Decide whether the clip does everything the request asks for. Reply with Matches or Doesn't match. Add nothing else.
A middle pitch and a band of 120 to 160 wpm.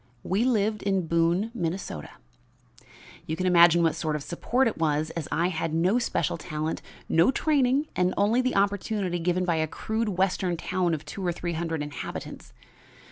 Doesn't match